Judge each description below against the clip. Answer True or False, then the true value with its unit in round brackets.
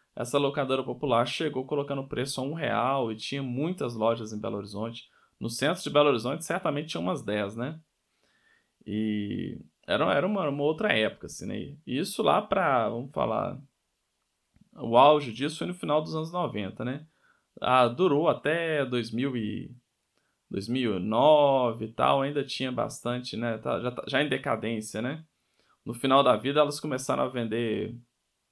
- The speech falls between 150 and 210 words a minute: True (165 wpm)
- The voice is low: True (130 Hz)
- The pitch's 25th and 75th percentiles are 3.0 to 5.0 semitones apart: True (4.3 semitones)